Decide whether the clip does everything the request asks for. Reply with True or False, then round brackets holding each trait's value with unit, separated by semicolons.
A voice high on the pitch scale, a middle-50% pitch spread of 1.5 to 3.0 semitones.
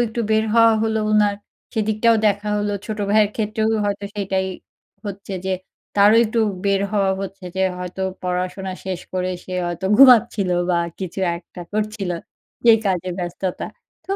True (200 Hz; 2.5 semitones)